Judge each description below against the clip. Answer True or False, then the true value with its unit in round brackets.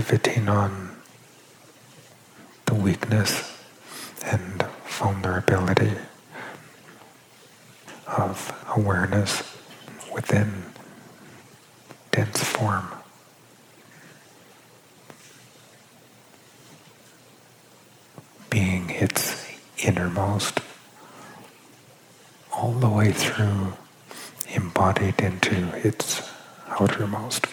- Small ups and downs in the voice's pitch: True (2.3 semitones)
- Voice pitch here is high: False (100 Hz)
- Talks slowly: True (50 wpm)